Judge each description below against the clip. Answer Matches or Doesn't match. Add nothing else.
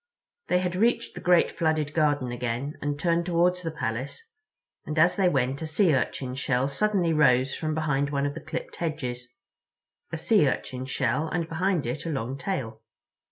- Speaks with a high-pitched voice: Doesn't match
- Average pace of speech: Matches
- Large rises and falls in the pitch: Doesn't match